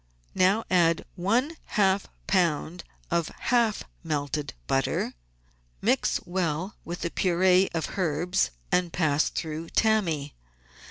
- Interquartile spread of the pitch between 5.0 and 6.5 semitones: No, average, 3.2 semitones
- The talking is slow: Yes, slow, 110 wpm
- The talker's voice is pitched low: No, medium, 175 Hz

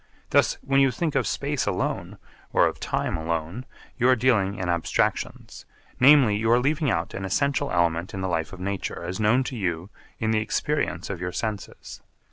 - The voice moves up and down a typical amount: No, wide, 6.4 semitones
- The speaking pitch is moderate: No, low, 105 Hz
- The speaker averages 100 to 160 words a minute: No, average, 190 wpm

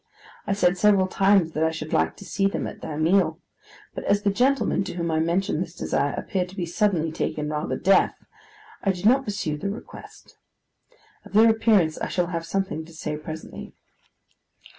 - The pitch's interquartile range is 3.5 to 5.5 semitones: Yes, average, 3.8 semitones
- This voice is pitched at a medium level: Yes, medium, 180 Hz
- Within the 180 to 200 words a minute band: Yes, average, 190 wpm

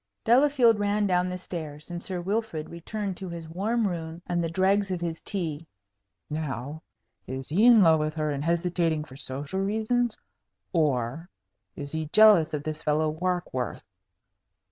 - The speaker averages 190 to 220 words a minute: No, average, 160 wpm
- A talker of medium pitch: Yes, medium, 170 Hz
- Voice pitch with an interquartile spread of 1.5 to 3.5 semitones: No, average, 4.3 semitones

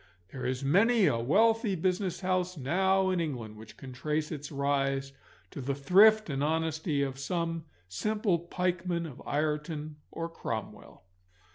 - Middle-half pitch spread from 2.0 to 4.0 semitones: No, average, 4.9 semitones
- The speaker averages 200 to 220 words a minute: No, average, 145 wpm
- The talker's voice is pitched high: No, medium, 160 Hz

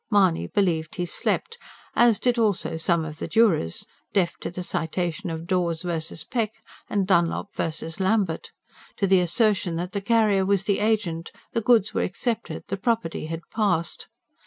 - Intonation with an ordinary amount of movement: Yes, average, 4.1 semitones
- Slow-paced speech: No, average, 165 wpm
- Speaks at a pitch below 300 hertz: Yes, high, 190 Hz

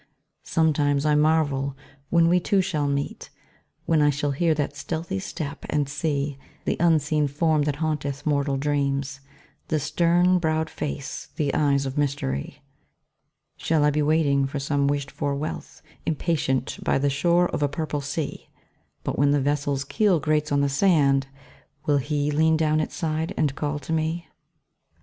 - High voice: No, medium, 145 Hz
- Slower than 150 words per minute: No, average, 165 wpm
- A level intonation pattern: Yes, narrow, 2.1 semitones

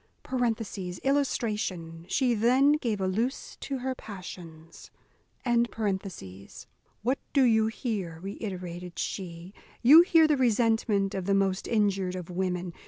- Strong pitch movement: No, average, 4.9 semitones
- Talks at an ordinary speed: No, slow, 115 wpm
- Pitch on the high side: Yes, high, 200 Hz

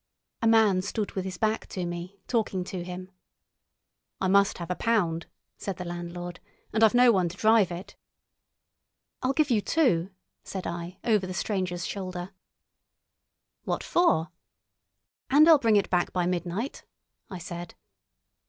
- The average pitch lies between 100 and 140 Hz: No, medium, 185 Hz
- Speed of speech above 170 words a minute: No, average, 155 wpm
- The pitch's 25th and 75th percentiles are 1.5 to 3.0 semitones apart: No, average, 3.8 semitones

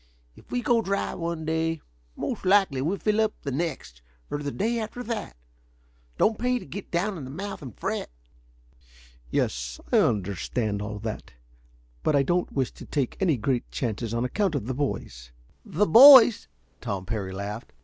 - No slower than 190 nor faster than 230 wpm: No, average, 175 wpm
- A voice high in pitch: No, medium, 150 Hz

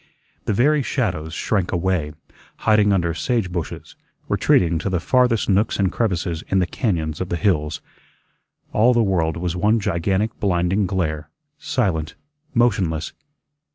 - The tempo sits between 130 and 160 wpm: Yes, average, 140 wpm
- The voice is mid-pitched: No, very low, 95 Hz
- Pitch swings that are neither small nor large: Yes, average, 4.1 semitones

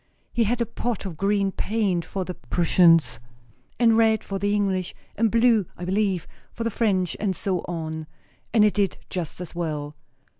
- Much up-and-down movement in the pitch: No, average, 3.8 semitones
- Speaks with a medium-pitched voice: No, high, 195 Hz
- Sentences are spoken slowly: No, average, 180 wpm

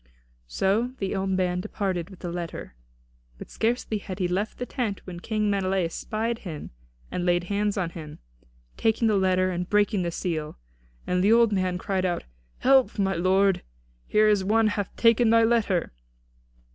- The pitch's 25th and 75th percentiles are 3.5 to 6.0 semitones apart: No, average, 3.1 semitones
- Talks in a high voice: Yes, high, 195 Hz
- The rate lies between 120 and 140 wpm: No, average, 170 wpm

